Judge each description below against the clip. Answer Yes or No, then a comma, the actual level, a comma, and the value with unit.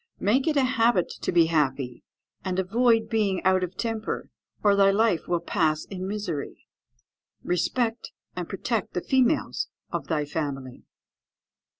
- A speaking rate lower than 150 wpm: Yes, average, 140 wpm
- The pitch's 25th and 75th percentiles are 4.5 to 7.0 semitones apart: Yes, wide, 5.4 semitones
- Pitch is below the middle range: No, high, 190 Hz